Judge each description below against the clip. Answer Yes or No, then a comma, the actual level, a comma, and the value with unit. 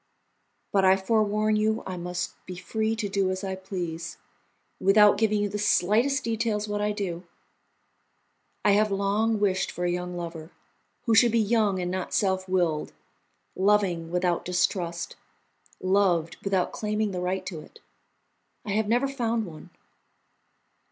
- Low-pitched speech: No, high, 195 Hz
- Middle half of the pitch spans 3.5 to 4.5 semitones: No, average, 3.0 semitones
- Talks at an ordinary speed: Yes, average, 150 wpm